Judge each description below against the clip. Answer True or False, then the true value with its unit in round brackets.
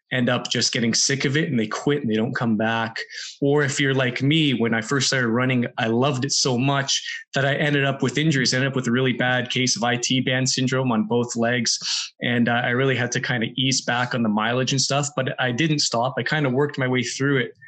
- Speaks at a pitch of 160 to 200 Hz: False (130 Hz)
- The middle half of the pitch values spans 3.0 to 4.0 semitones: False (2.4 semitones)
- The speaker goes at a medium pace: False (265 wpm)